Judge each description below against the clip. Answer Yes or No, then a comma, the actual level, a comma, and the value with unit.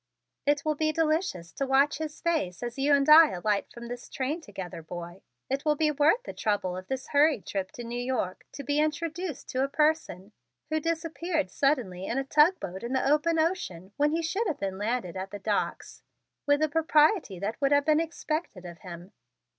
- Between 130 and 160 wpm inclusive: No, average, 200 wpm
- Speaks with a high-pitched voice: Yes, very high, 280 Hz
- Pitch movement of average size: No, wide, 7.4 semitones